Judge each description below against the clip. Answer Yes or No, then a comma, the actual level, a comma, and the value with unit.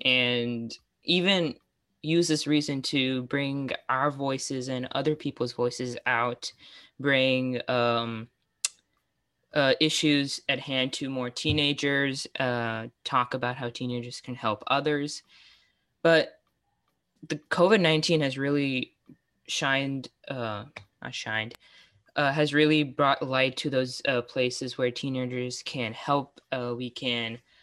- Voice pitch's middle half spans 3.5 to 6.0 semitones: No, average, 2.8 semitones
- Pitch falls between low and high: No, low, 130 Hz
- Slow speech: Yes, slow, 125 wpm